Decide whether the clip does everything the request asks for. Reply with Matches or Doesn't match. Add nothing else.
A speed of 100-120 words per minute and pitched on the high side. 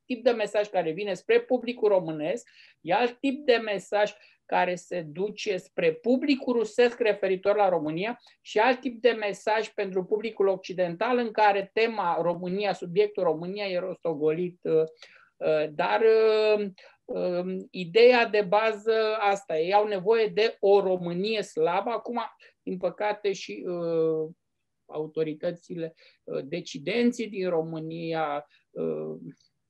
Matches